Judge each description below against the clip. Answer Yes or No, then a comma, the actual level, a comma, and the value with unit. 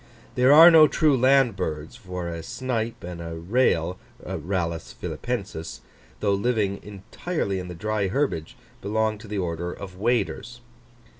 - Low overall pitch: Yes, low, 100 Hz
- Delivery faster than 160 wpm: No, average, 145 wpm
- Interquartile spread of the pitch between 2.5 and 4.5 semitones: No, wide, 5.5 semitones